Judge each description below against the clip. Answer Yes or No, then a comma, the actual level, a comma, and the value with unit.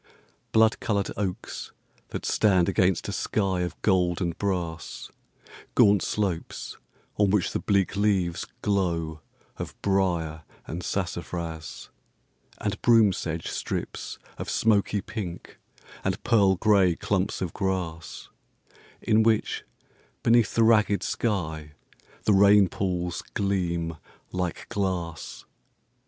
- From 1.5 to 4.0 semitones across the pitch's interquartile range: Yes, average, 3.1 semitones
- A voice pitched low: Yes, very low, 95 Hz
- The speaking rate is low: Yes, slow, 115 wpm